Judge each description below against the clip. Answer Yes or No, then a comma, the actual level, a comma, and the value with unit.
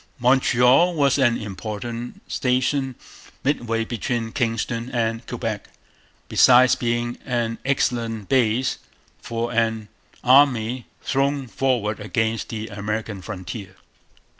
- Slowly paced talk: Yes, slow, 100 wpm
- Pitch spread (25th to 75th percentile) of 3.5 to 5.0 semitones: No, narrow, 2.5 semitones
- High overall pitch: No, low, 120 Hz